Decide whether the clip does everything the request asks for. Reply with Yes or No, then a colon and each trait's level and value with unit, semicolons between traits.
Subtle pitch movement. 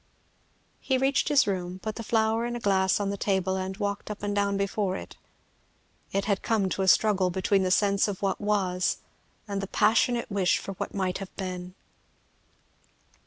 Yes: narrow, 1.9 semitones